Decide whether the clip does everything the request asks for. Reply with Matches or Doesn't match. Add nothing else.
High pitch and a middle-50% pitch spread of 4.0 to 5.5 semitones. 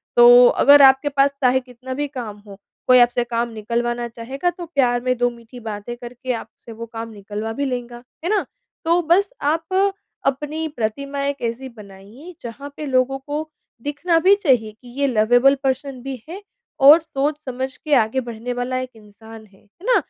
Doesn't match